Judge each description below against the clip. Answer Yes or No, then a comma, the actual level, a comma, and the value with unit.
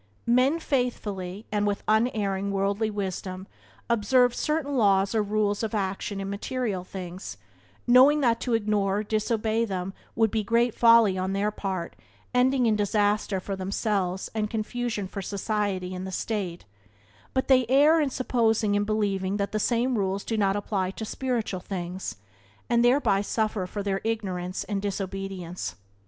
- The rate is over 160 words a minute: No, average, 155 wpm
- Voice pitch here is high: Yes, high, 205 Hz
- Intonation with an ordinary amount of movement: Yes, average, 3.0 semitones